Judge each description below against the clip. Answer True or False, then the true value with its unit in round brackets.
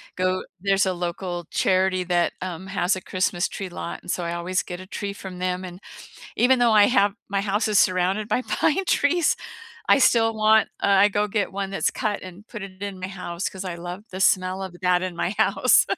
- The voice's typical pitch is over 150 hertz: True (190 Hz)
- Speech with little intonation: True (2.1 semitones)